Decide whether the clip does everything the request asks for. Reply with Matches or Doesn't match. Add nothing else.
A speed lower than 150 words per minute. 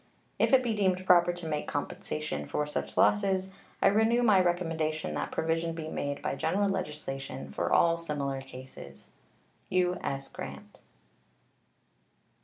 Matches